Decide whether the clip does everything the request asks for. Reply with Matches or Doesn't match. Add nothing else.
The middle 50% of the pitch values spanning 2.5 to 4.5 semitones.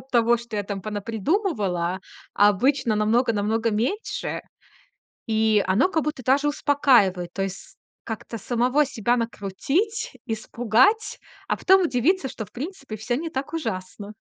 Doesn't match